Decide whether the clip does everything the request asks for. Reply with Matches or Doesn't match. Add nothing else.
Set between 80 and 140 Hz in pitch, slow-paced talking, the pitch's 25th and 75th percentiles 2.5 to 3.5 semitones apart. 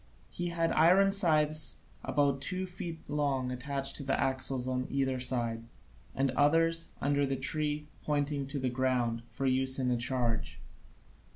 Doesn't match